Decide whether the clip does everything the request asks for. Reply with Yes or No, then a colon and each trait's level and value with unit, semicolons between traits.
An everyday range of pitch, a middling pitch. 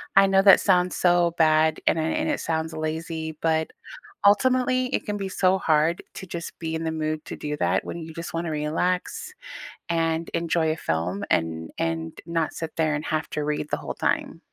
No: narrow, 2.1 semitones; medium, 160 Hz